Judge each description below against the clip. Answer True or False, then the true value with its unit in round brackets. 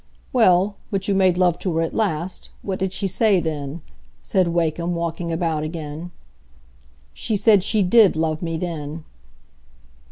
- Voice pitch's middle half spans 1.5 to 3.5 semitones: True (3.0 semitones)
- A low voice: False (175 Hz)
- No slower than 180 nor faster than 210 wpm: False (155 wpm)